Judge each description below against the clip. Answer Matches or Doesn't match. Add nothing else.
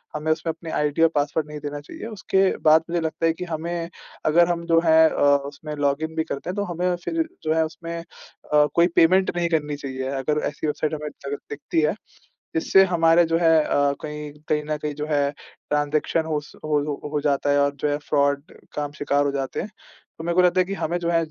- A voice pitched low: Doesn't match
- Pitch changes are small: Matches